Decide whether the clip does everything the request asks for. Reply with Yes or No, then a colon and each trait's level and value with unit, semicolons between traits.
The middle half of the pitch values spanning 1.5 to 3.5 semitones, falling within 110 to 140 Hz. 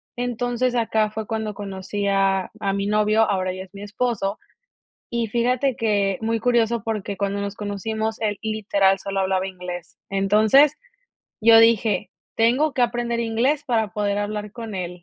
No: average, 2.7 semitones; high, 215 Hz